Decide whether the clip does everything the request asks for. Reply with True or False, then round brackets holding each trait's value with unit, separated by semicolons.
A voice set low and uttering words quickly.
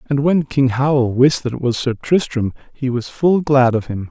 True (130 Hz; 235 wpm)